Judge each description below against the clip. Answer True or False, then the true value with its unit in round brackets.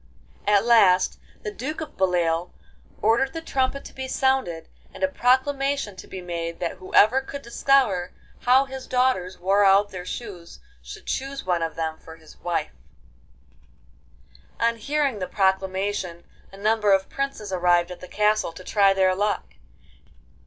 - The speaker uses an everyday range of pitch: False (6.4 semitones)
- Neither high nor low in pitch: False (205 Hz)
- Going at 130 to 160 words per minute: True (155 wpm)